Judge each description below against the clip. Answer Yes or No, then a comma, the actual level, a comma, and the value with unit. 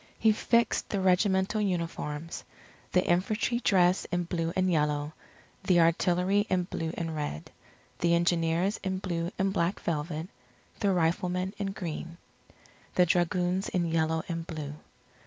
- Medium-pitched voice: Yes, medium, 175 Hz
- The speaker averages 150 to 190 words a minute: No, average, 140 wpm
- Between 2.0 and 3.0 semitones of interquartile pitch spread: Yes, narrow, 2.4 semitones